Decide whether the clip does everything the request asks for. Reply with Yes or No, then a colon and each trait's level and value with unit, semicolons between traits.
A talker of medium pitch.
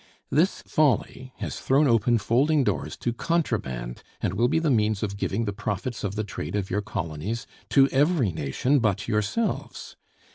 No: low, 115 Hz